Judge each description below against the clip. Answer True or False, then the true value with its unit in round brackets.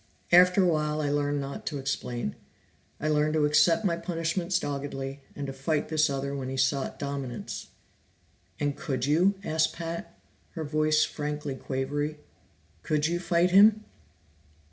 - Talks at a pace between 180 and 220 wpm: False (150 wpm)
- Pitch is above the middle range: False (150 Hz)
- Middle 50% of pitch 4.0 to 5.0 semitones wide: False (3.0 semitones)